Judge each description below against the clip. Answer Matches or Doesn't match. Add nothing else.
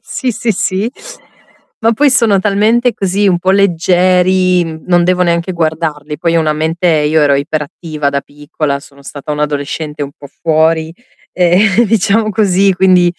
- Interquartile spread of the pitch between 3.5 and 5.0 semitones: Matches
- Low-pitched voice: Doesn't match